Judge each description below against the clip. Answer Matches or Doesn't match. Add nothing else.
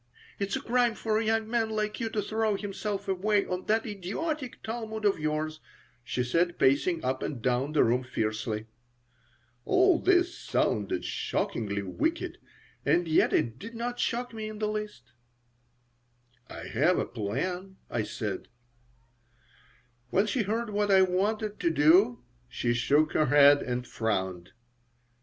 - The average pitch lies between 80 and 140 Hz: Doesn't match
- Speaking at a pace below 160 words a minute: Matches